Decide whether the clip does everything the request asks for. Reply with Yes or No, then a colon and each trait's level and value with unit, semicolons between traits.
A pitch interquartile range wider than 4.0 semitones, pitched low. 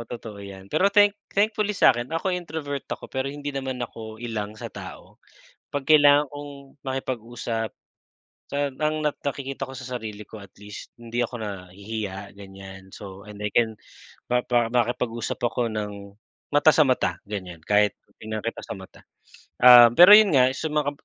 Yes: wide, 5.5 semitones; low, 120 Hz